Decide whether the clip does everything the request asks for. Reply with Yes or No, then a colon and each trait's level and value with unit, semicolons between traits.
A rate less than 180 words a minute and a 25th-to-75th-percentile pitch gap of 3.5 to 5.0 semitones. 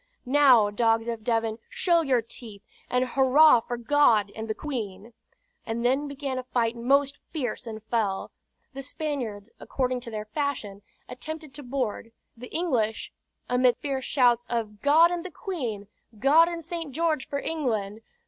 Yes: average, 160 wpm; average, 4.3 semitones